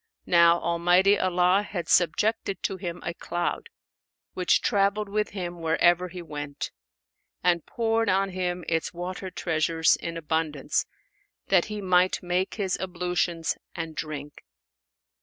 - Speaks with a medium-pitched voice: Yes, medium, 180 Hz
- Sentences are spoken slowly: Yes, slow, 130 wpm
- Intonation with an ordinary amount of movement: No, narrow, 2.1 semitones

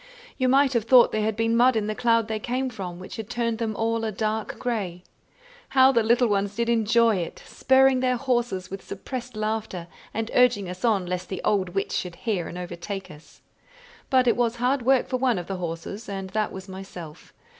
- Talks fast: Yes, fast, 210 wpm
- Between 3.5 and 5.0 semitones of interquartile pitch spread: Yes, average, 4.0 semitones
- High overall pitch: Yes, high, 220 Hz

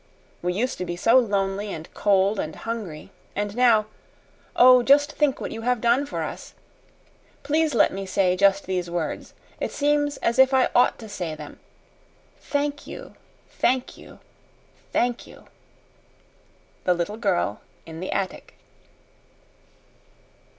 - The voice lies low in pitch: No, high, 215 Hz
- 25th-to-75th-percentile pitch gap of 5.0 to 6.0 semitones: Yes, wide, 5.4 semitones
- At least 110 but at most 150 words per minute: Yes, average, 145 wpm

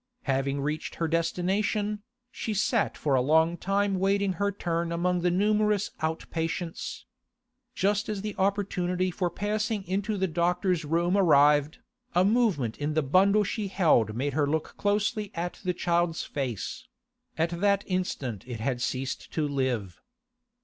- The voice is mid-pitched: Yes, medium, 175 Hz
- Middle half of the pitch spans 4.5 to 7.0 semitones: Yes, average, 4.8 semitones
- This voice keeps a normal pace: Yes, average, 150 wpm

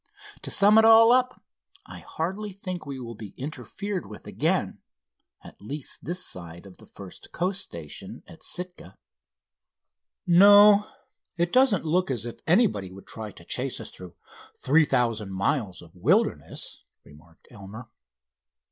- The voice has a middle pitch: Yes, medium, 150 Hz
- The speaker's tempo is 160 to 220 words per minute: No, average, 140 wpm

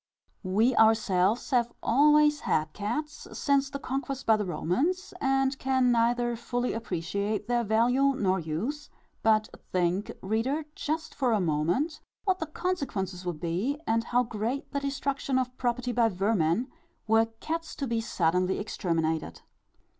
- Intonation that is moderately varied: No, wide, 5.9 semitones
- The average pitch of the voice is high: Yes, high, 235 Hz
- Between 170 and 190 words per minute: No, average, 145 wpm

